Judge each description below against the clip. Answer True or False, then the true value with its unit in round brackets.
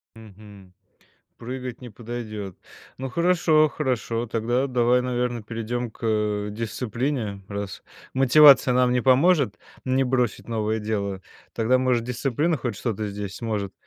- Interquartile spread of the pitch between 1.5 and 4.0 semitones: True (3.2 semitones)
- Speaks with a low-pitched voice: True (120 Hz)